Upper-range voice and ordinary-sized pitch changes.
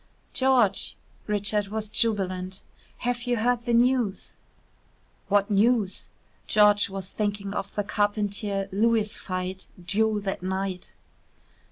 No: high, 205 Hz; narrow, 2.2 semitones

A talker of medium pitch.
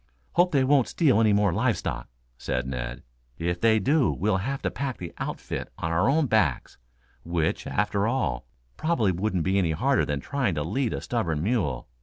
No: low, 100 Hz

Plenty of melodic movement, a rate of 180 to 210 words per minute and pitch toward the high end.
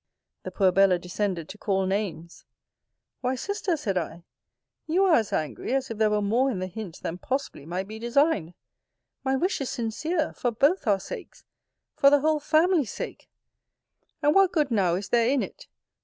Yes: wide, 7.2 semitones; average, 185 wpm; high, 230 Hz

